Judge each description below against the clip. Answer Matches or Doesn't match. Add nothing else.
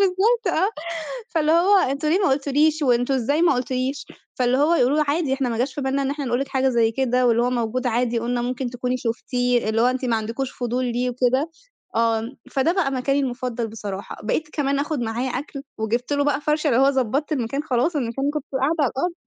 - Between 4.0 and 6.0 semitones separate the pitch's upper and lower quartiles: Doesn't match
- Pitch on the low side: Doesn't match